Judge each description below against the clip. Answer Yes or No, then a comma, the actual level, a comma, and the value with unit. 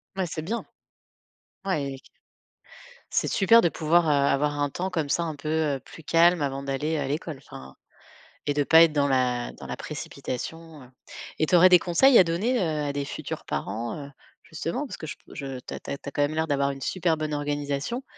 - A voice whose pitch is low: No, medium, 150 Hz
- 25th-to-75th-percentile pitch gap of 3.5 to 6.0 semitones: No, average, 3.1 semitones